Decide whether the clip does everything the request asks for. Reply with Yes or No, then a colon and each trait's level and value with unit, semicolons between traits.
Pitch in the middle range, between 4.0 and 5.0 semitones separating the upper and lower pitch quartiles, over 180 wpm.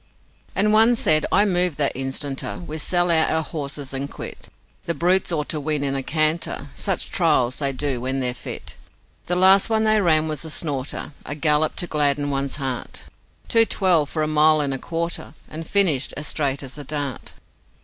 No: medium, 155 Hz; average, 3.6 semitones; average, 195 wpm